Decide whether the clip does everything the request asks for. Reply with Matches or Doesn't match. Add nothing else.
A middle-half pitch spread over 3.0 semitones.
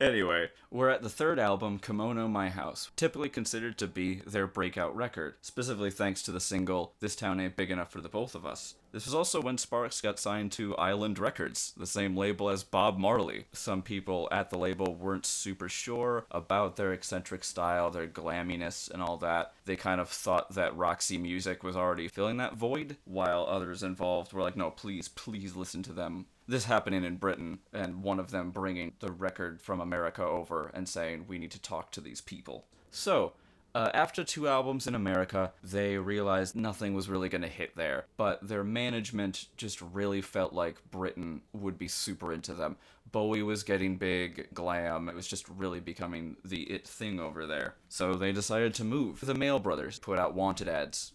Doesn't match